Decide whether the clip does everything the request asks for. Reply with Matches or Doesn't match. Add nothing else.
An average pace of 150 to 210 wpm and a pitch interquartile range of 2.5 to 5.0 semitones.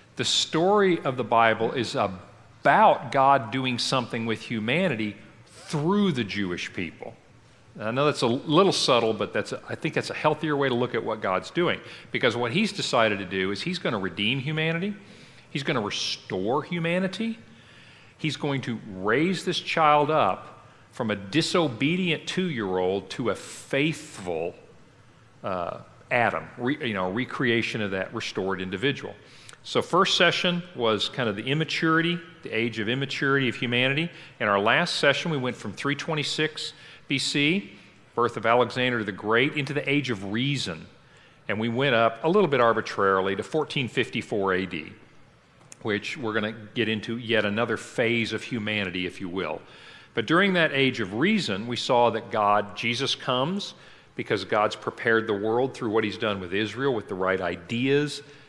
Doesn't match